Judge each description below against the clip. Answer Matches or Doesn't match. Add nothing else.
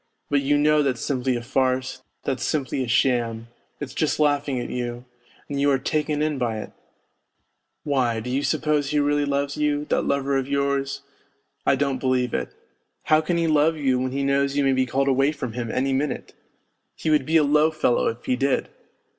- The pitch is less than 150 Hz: Matches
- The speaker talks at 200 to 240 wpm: Matches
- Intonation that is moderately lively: Doesn't match